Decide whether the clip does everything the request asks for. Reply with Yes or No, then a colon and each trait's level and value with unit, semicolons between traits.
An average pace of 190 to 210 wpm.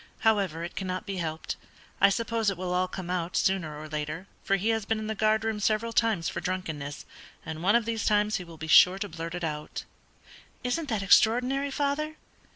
Yes: fast, 205 wpm